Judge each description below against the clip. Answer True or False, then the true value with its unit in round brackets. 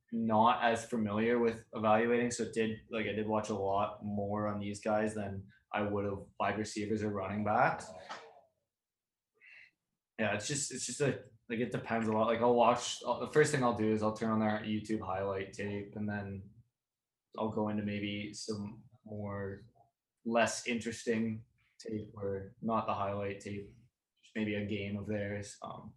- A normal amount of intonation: False (2.0 semitones)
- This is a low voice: True (110 Hz)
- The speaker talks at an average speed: True (180 wpm)